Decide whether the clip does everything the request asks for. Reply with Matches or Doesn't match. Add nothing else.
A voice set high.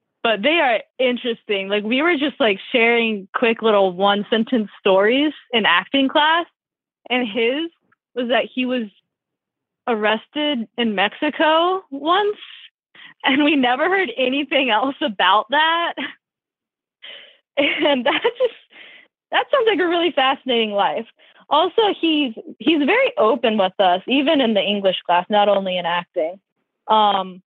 Matches